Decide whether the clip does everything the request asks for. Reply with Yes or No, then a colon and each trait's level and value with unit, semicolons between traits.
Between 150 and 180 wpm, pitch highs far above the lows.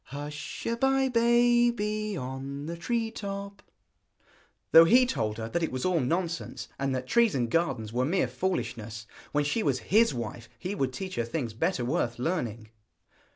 Yes: average, 170 wpm; wide, 8.9 semitones